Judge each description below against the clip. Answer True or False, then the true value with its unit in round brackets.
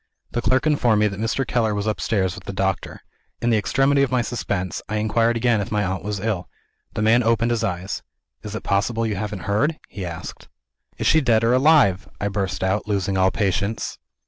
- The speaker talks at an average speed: False (210 wpm)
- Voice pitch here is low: True (110 Hz)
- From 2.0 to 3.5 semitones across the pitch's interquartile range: True (3.2 semitones)